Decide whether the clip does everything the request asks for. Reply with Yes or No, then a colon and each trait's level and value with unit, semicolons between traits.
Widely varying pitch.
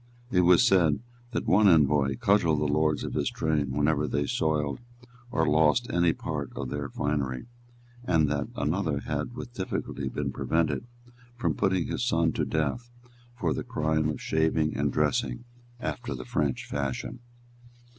No: average, 4.2 semitones